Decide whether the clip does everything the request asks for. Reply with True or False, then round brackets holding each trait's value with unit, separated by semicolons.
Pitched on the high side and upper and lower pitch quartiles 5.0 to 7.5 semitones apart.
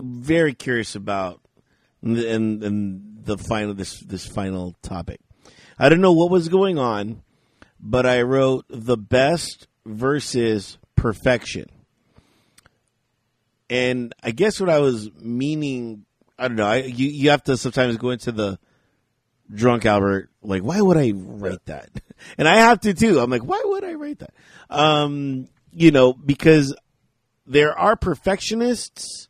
False (125 Hz; 5.6 semitones)